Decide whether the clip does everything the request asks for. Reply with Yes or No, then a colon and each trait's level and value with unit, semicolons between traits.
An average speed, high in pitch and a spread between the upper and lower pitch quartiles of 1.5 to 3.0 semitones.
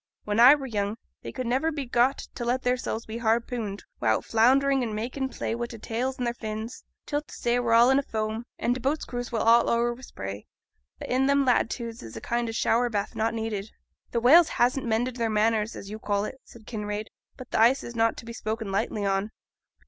No: fast, 230 wpm; high, 235 Hz; narrow, 2.4 semitones